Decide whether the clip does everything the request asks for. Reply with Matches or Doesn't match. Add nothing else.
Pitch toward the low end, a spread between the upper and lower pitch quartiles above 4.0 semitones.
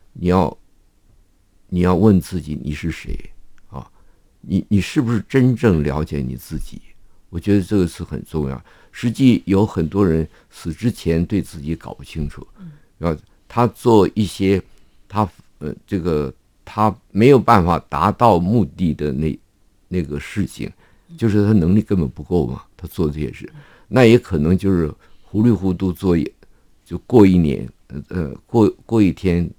Matches